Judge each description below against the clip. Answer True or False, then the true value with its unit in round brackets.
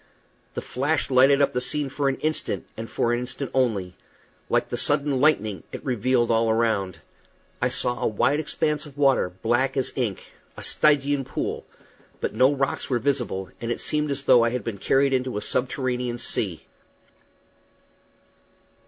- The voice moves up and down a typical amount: True (3.3 semitones)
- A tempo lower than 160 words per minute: False (170 wpm)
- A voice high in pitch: False (130 Hz)